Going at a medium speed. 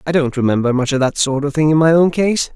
No: fast, 305 wpm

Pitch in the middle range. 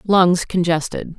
Yes: medium, 175 Hz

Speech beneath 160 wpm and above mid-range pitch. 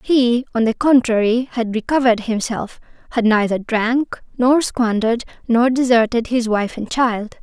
Yes: average, 145 wpm; high, 235 Hz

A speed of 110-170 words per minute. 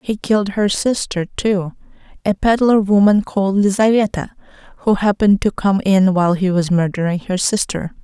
Yes: average, 155 wpm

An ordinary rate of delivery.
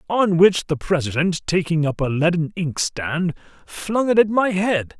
Yes: average, 170 wpm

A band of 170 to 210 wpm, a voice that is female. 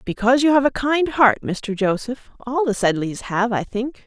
Yes: fast, 205 wpm; female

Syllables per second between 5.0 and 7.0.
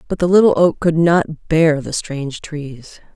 No: 4.2 syllables/s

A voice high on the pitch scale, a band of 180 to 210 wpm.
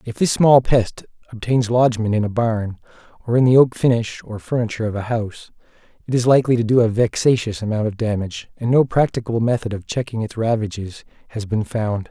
No: low, 115 Hz; average, 200 wpm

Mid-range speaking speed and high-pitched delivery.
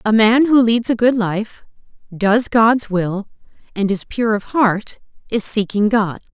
Yes: average, 170 wpm; high, 215 Hz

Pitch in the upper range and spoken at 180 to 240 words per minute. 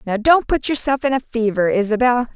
Yes: high, 240 Hz; fast, 205 wpm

